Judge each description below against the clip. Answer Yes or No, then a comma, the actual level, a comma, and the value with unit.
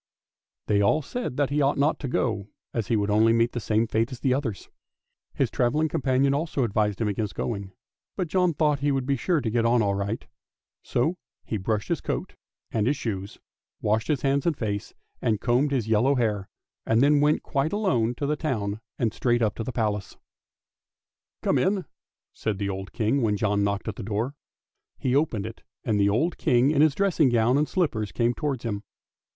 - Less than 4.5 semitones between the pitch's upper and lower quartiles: No, average, 5.0 semitones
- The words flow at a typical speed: No, fast, 210 wpm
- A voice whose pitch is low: Yes, low, 120 Hz